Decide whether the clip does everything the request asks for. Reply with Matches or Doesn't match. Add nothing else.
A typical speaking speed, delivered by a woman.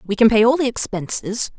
Doesn't match